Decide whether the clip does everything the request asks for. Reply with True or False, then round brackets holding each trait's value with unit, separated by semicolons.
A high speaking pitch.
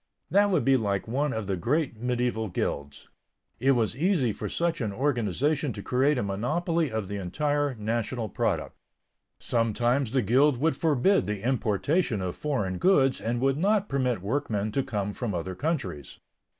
False (125 Hz)